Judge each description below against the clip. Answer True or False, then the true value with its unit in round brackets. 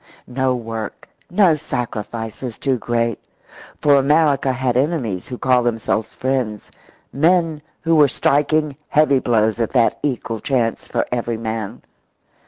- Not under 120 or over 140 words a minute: True (135 wpm)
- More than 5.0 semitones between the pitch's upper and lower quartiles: False (4.1 semitones)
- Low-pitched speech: True (125 Hz)